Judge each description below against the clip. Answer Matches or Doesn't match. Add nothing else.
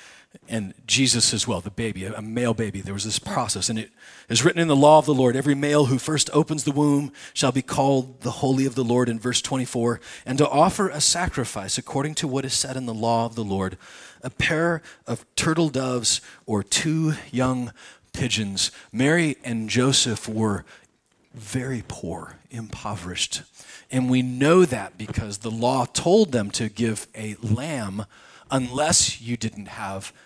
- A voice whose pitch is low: Matches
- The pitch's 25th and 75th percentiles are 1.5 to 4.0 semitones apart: Doesn't match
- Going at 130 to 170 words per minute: Doesn't match